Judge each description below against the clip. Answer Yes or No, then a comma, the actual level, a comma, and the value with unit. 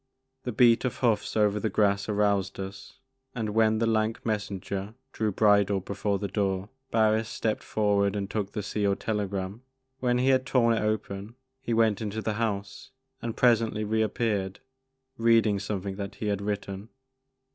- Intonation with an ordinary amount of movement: No, narrow, 2.0 semitones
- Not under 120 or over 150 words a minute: No, average, 165 wpm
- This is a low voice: Yes, low, 105 Hz